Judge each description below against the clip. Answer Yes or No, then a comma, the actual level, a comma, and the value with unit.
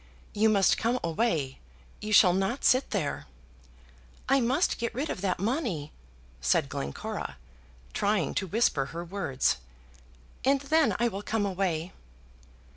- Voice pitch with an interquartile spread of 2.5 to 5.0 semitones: No, wide, 5.6 semitones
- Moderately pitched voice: No, high, 200 Hz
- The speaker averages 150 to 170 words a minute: No, slow, 135 wpm